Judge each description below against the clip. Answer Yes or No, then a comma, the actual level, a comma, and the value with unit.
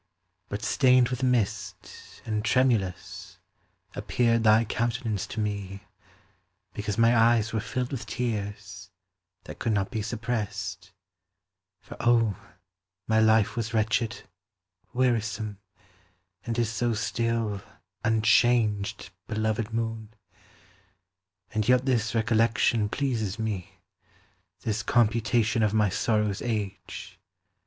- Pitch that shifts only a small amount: Yes, narrow, 2.0 semitones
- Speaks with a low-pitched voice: Yes, low, 110 Hz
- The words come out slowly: Yes, slow, 105 wpm